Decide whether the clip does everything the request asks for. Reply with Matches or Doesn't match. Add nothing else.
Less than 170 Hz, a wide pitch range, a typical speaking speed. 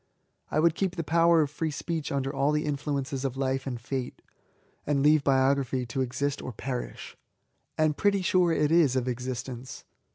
Doesn't match